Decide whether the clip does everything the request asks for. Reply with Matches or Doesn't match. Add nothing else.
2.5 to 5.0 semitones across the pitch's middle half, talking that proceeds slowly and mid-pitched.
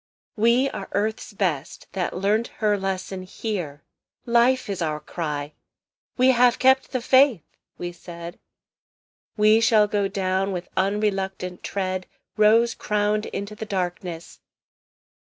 Doesn't match